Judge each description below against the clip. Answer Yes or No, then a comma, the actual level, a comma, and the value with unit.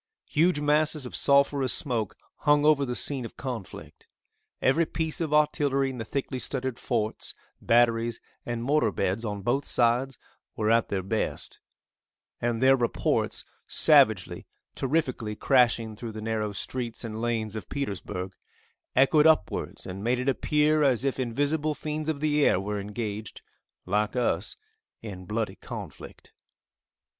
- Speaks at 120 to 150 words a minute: Yes, average, 145 wpm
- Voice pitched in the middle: No, low, 125 Hz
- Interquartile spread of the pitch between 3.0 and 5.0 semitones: Yes, average, 4.5 semitones